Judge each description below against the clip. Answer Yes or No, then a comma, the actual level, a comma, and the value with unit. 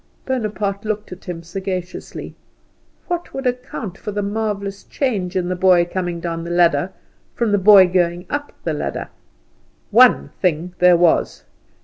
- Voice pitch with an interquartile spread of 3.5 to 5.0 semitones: No, average, 3.1 semitones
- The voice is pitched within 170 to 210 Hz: Yes, medium, 185 Hz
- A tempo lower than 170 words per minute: Yes, average, 150 wpm